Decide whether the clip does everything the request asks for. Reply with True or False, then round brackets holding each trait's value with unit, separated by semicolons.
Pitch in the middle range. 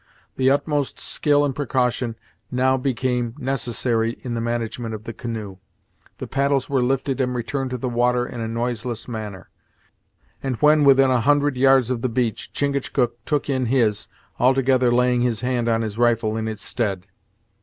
False (125 Hz)